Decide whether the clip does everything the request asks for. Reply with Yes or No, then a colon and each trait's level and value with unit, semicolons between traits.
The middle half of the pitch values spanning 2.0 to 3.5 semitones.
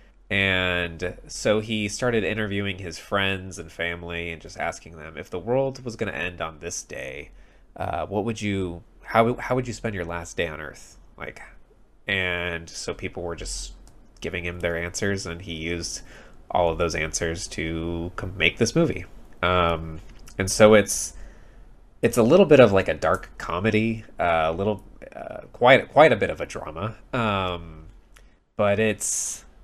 No: average, 4.1 semitones